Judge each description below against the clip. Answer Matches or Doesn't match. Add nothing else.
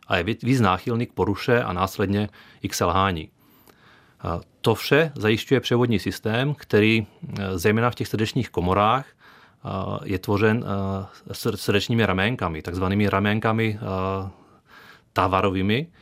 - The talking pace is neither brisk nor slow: Doesn't match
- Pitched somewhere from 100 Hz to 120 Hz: Matches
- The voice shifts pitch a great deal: Doesn't match